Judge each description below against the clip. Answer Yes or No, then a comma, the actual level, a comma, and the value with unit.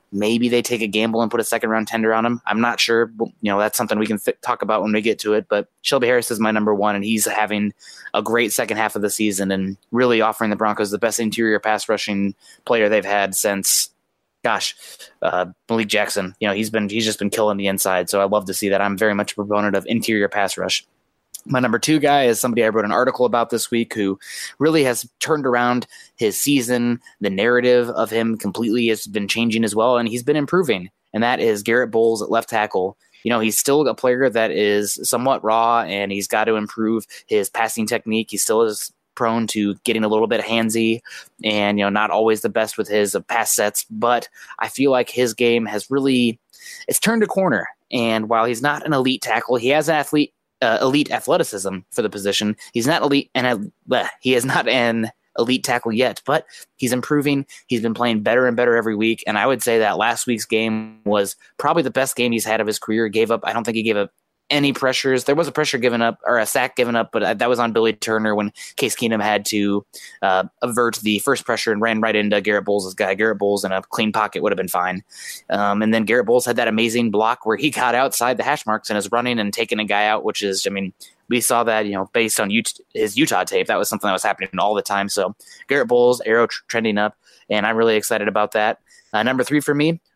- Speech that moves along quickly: Yes, fast, 245 wpm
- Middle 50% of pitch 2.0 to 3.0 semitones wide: Yes, narrow, 2.6 semitones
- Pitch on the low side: Yes, low, 115 Hz